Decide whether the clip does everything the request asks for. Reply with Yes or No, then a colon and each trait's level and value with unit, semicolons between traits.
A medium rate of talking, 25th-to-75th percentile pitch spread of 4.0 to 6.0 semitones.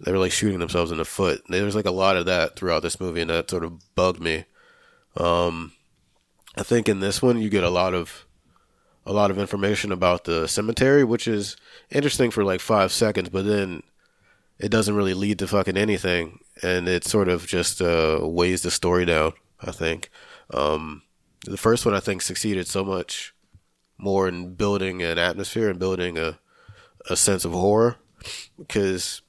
No: average, 190 wpm; average, 2.9 semitones